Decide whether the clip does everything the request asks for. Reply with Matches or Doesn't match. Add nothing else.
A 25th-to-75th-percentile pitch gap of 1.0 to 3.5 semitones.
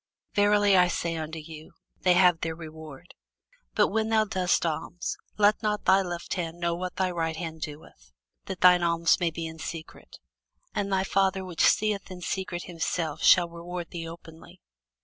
Matches